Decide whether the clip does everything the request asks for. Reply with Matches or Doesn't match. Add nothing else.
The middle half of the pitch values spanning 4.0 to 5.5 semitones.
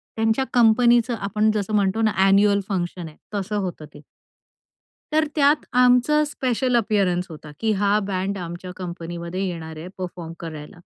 Matches